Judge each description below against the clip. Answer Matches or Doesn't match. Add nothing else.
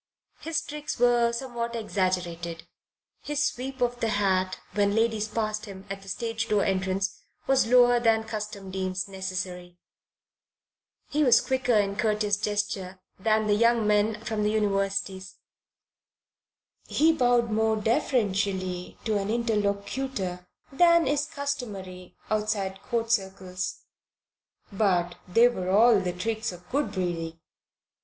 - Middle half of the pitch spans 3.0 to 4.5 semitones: Matches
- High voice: Matches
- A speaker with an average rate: Doesn't match